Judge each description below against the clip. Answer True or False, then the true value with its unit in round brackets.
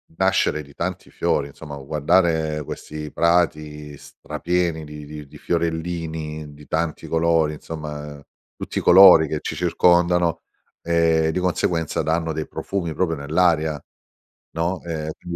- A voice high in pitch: False (80 Hz)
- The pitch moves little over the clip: True (1.9 semitones)